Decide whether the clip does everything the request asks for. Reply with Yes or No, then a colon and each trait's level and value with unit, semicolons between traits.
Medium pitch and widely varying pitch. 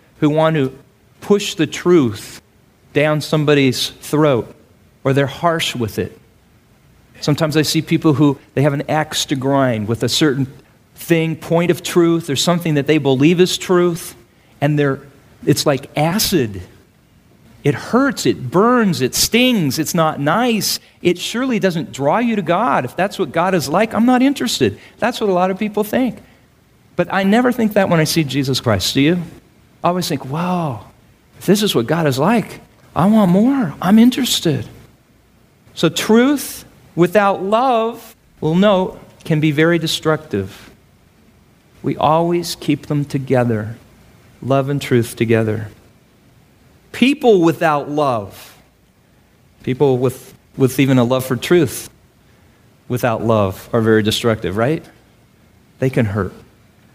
Yes: medium, 150 Hz; wide, 5.9 semitones